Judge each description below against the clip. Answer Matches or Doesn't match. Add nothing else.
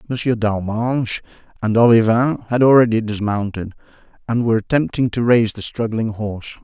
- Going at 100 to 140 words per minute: Matches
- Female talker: Doesn't match